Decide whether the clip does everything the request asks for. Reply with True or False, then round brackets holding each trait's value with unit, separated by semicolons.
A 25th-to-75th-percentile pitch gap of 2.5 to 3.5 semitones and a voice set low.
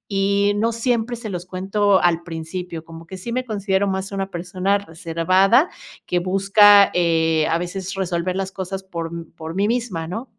False (2.8 semitones; 190 Hz)